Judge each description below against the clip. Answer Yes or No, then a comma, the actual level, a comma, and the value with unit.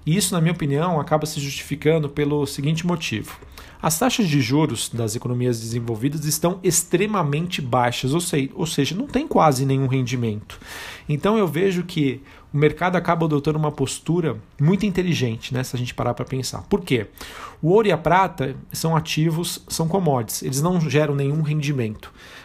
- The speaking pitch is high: No, medium, 150 Hz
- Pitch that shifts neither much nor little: Yes, average, 4.8 semitones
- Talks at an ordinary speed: Yes, average, 170 wpm